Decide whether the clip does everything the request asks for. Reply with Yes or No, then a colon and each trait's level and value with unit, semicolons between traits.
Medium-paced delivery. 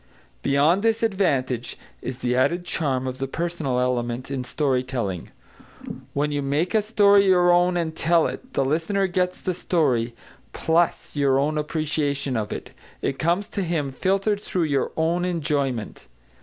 Yes: average, 155 wpm